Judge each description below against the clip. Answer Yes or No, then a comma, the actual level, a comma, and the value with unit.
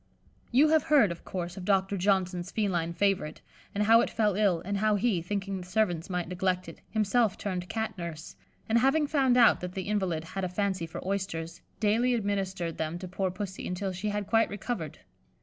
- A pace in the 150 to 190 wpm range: No, average, 200 wpm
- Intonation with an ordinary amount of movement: Yes, average, 3.0 semitones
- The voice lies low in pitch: No, high, 195 Hz